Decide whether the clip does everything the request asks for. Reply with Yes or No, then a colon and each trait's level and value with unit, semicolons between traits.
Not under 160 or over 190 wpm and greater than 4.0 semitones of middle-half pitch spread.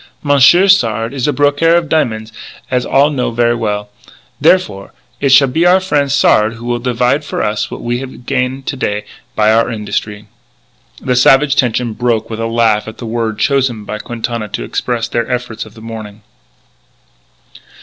No: average, 180 wpm; average, 3.7 semitones